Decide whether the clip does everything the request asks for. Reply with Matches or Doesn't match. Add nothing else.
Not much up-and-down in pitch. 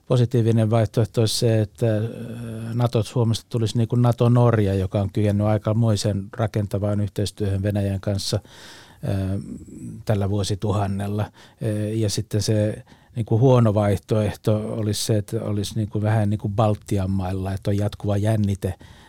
Matches